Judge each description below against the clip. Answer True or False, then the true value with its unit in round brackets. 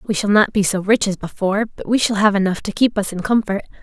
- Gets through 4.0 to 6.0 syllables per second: False (6.2 syllables/s)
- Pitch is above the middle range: True (205 Hz)